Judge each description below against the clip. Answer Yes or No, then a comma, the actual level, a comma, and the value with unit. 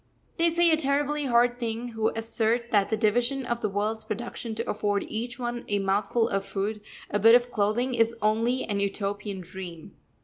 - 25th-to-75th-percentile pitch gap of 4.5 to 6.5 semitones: No, average, 2.9 semitones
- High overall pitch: Yes, high, 225 Hz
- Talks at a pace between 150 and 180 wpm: No, average, 190 wpm